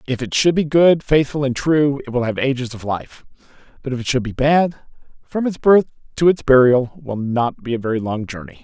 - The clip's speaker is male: Yes, male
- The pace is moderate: No, fast, 230 wpm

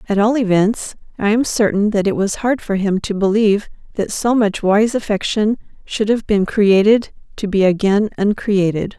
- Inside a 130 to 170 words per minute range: No, average, 180 wpm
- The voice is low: No, high, 205 Hz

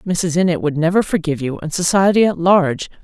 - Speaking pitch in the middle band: Yes, medium, 170 Hz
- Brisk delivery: No, average, 195 wpm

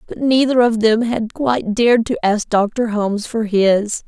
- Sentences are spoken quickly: No, average, 190 wpm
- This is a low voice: No, high, 225 Hz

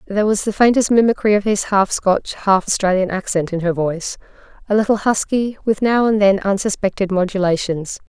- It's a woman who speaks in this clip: Yes, female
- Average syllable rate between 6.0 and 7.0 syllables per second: No, 5.5 syllables/s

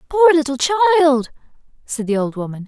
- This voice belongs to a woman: Yes, female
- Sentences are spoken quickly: No, average, 155 wpm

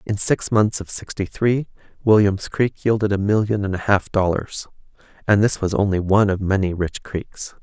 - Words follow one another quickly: No, average, 190 wpm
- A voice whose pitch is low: Yes, low, 100 Hz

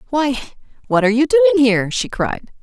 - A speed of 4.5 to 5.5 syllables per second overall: No, 5.8 syllables/s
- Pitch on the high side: Yes, high, 235 Hz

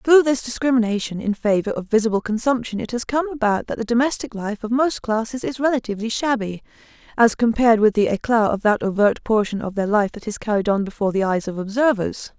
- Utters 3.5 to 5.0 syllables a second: No, 6.1 syllables/s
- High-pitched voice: Yes, high, 225 Hz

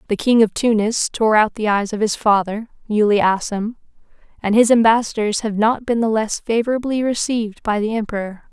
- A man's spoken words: No, female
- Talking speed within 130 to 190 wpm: Yes, average, 185 wpm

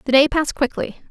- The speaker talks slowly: No, fast, 215 wpm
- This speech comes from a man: No, female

